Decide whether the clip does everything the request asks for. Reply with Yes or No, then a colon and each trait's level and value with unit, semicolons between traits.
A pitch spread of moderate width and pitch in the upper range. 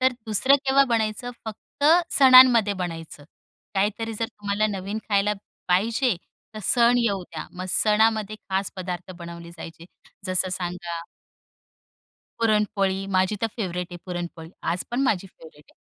Yes: average, 3.9 semitones; high, 200 Hz